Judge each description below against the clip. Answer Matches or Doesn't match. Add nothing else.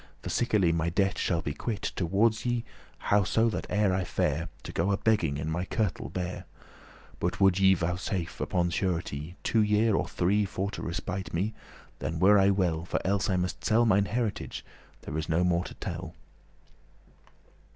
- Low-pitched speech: Matches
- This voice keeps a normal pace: Matches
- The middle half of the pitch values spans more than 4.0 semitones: Doesn't match